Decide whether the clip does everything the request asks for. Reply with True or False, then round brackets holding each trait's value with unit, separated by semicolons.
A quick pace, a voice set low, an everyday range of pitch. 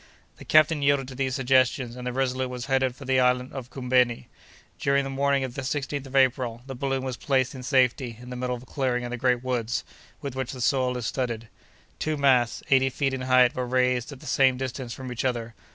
False (230 wpm; 130 Hz; 1.3 semitones)